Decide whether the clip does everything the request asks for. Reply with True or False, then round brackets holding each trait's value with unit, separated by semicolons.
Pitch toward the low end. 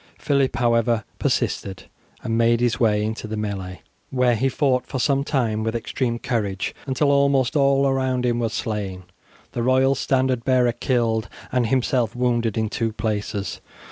True (120 Hz)